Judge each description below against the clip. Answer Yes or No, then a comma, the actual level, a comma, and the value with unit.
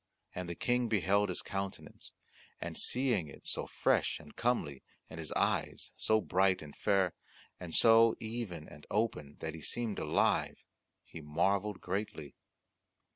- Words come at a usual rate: Yes, average, 145 wpm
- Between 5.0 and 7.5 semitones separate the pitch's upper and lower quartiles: Yes, average, 5.3 semitones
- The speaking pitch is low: Yes, very low, 95 Hz